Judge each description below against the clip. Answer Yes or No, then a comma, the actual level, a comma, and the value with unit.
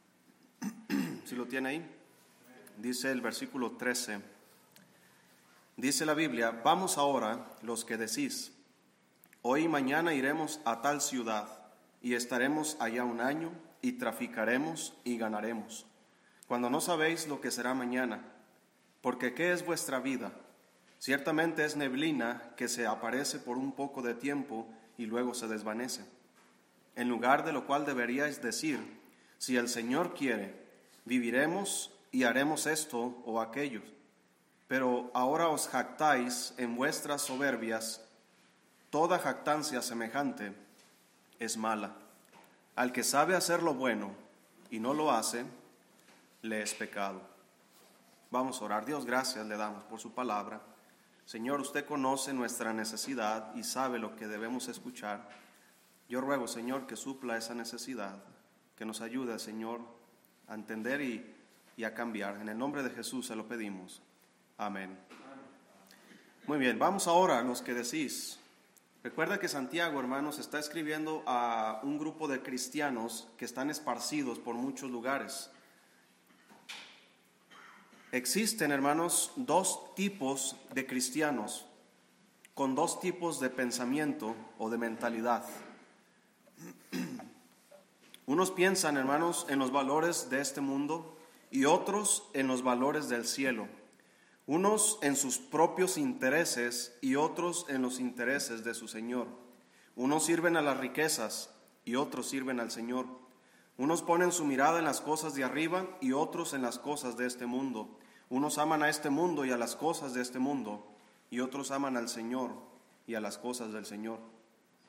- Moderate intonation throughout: Yes, average, 4.5 semitones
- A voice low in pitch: Yes, low, 130 Hz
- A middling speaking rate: Yes, average, 140 wpm